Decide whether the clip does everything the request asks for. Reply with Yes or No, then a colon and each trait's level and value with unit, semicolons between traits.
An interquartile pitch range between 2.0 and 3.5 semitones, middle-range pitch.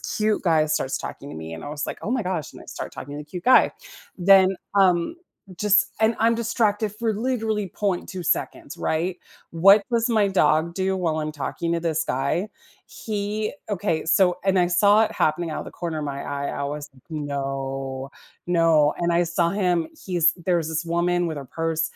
No: average, 4.5 semitones; medium, 175 Hz